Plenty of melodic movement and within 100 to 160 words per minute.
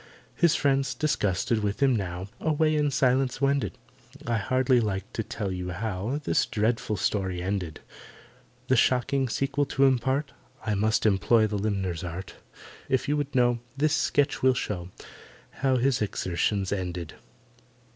Yes: wide, 5.7 semitones; average, 145 wpm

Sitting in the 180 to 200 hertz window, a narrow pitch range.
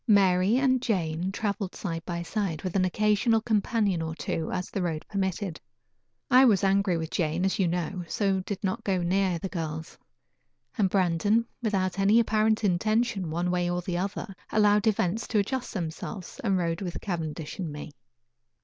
No: high, 190 Hz; average, 3.3 semitones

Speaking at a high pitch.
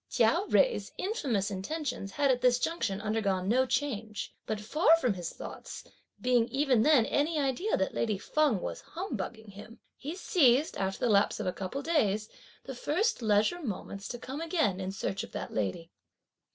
Yes: high, 240 Hz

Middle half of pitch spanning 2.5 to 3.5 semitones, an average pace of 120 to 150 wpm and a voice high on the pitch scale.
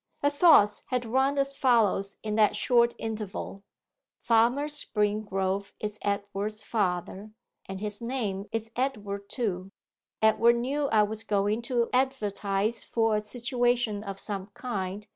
Yes: average, 3.1 semitones; slow, 135 wpm; high, 215 Hz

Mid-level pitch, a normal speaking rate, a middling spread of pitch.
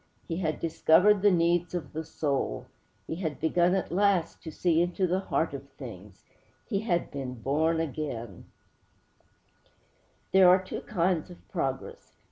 Yes: medium, 170 Hz; average, 150 wpm; average, 3.0 semitones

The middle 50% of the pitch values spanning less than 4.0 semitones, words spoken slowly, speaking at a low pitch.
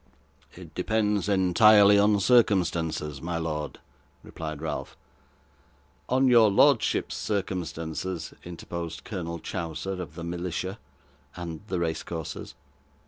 Yes: average, 3.6 semitones; slow, 105 wpm; very low, 90 Hz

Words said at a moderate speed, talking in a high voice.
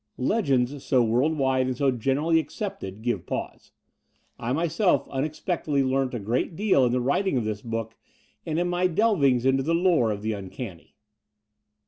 No: average, 165 wpm; low, 135 Hz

